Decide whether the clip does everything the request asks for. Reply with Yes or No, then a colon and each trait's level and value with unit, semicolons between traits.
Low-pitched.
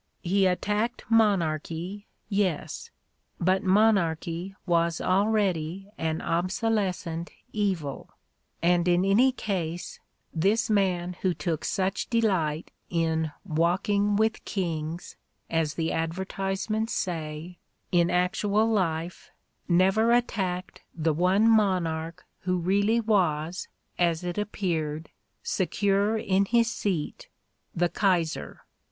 No: medium, 185 Hz